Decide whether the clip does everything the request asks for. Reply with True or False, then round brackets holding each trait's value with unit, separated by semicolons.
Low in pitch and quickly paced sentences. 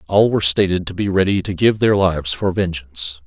True (90 Hz; 220 wpm)